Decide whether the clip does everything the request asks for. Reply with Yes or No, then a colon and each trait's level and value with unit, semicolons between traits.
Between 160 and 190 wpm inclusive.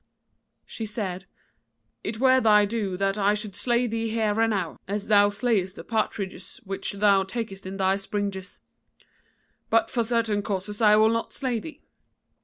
Yes: average, 165 wpm